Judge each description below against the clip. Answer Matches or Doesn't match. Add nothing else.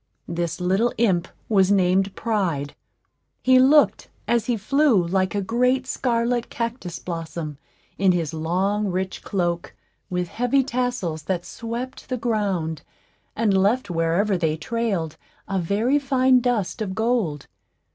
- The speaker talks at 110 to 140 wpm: Matches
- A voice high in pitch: Matches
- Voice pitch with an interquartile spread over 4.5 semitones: Matches